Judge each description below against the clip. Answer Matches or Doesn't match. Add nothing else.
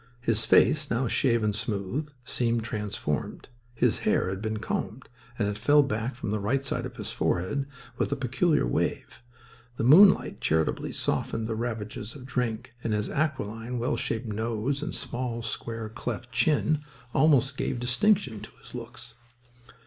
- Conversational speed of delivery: Matches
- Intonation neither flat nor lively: Matches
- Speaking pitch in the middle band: Doesn't match